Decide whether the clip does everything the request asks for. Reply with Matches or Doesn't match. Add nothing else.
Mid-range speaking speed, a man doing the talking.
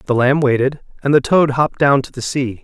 Doesn't match